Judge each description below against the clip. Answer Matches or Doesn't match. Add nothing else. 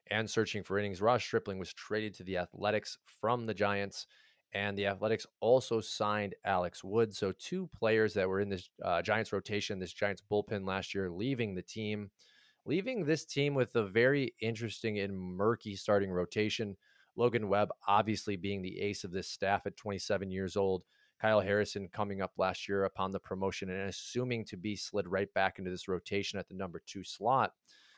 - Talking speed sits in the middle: Matches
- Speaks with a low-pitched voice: Matches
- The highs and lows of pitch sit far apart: Doesn't match